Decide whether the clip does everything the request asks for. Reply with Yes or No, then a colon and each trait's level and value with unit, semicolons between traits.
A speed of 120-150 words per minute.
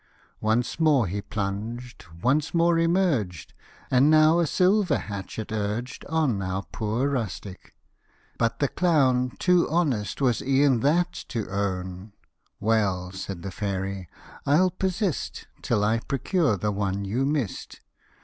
Yes: average, 140 wpm